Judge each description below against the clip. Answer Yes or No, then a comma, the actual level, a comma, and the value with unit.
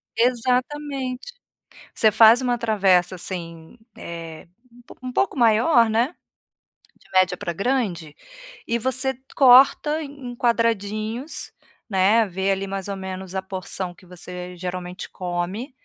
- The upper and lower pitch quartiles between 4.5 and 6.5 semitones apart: Yes, average, 5.2 semitones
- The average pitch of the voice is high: Yes, high, 215 Hz